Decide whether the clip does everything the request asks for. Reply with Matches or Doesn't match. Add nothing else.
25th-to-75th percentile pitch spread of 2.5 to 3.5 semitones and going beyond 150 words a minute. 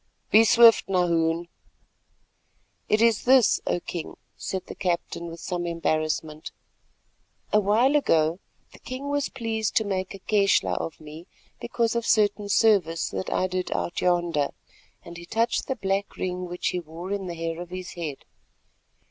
Doesn't match